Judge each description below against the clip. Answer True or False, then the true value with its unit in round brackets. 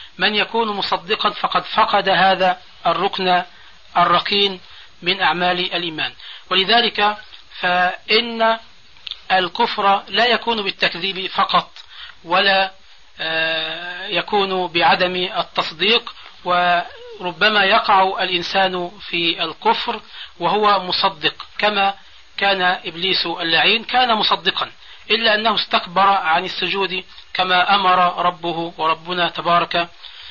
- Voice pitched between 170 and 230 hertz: True (185 Hz)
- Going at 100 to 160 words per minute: False (90 wpm)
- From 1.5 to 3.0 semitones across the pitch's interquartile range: True (2.6 semitones)